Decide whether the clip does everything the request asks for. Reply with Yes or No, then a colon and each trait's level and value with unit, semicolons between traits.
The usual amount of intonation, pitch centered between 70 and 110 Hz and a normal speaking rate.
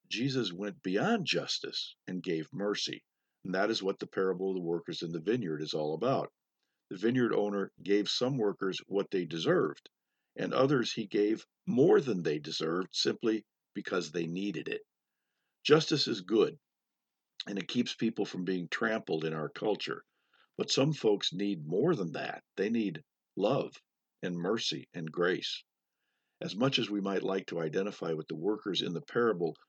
Yes: average, 4.6 semitones; low, 100 Hz; average, 170 wpm